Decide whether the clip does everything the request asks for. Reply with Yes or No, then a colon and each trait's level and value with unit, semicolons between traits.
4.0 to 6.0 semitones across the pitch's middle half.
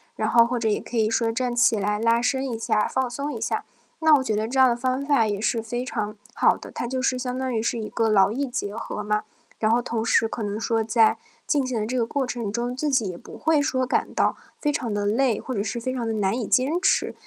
No: average, 2.9 semitones